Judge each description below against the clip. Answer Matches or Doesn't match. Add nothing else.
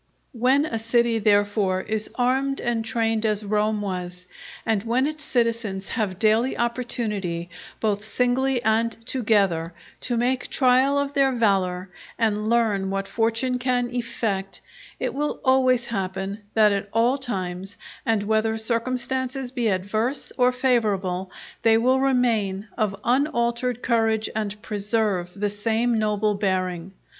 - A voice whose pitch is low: Doesn't match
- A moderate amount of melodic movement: Matches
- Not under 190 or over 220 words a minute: Doesn't match